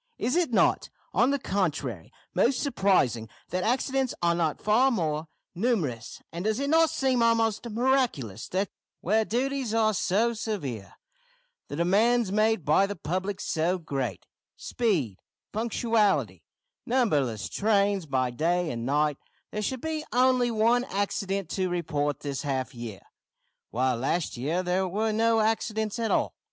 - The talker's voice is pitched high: Yes, high, 200 Hz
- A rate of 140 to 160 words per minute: Yes, average, 145 wpm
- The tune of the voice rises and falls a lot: Yes, wide, 7.2 semitones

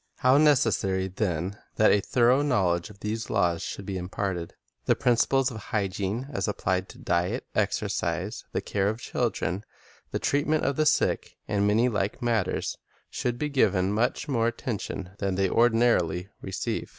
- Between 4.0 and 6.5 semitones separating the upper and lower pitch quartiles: Yes, average, 4.3 semitones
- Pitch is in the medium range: No, low, 105 Hz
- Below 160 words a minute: No, average, 165 wpm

